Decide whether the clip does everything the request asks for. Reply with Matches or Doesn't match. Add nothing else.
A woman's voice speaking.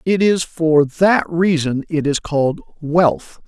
Doesn't match